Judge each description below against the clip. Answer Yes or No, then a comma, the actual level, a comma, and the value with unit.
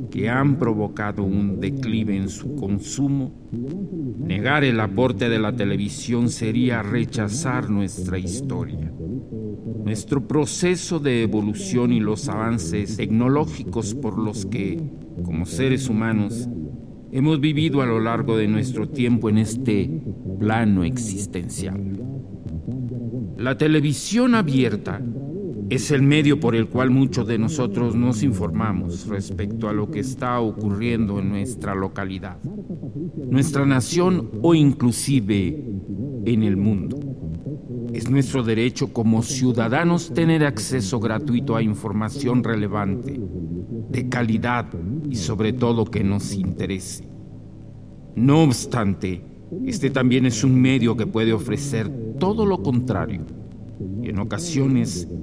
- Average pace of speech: No, slow, 120 wpm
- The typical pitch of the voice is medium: No, low, 115 Hz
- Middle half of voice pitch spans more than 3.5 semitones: Yes, average, 4.2 semitones